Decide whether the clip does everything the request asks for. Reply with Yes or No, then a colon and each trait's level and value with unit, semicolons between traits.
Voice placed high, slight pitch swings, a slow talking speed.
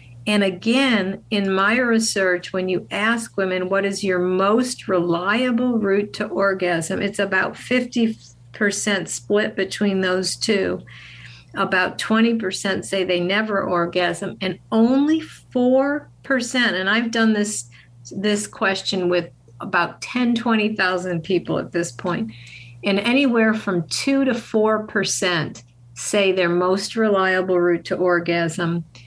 No: high, 195 Hz; average, 3.8 semitones; slow, 125 wpm